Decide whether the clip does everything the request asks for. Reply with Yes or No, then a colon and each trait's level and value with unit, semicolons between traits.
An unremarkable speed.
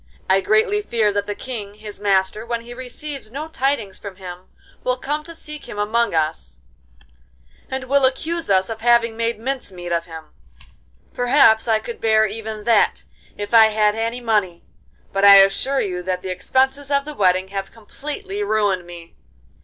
Yes: average, 175 wpm